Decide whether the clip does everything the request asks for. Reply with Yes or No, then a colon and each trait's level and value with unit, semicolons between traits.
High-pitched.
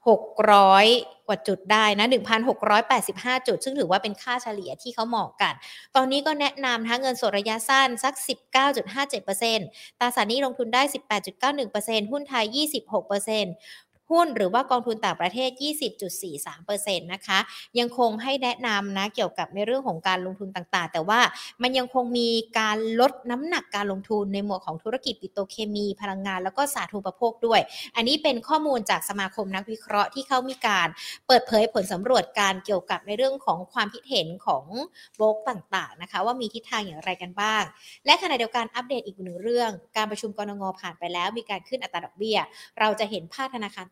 Yes: high, 220 Hz